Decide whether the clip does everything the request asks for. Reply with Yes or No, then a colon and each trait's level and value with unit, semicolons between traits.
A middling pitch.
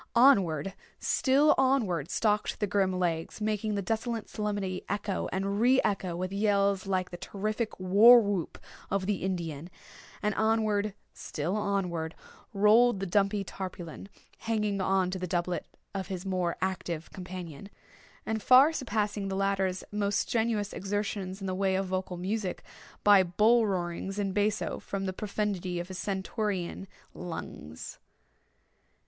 No: high, 195 Hz